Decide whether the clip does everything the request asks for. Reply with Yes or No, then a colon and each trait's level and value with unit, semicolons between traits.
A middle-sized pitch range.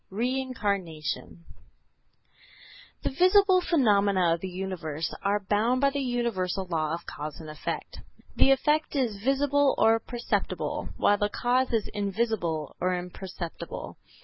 No: wide, 6.2 semitones